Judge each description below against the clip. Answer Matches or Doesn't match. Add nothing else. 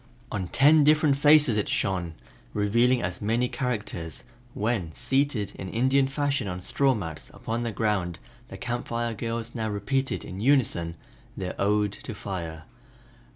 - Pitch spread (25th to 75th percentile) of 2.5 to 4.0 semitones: Doesn't match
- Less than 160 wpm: Matches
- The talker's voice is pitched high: Doesn't match